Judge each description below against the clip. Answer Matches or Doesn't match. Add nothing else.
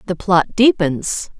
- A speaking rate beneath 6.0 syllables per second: Matches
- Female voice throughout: Matches